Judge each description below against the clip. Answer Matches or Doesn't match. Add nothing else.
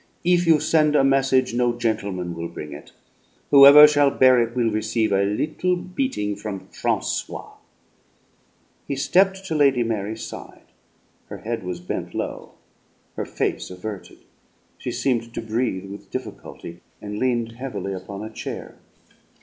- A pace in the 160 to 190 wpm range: Doesn't match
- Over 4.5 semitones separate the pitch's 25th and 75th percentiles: Matches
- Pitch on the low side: Matches